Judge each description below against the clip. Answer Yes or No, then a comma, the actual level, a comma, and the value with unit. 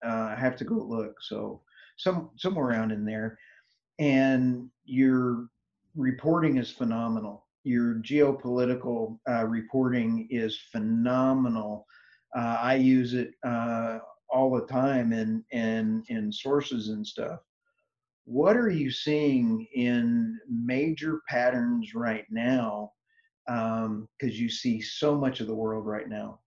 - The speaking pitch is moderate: No, low, 125 Hz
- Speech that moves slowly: Yes, slow, 130 wpm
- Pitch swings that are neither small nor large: Yes, average, 4.5 semitones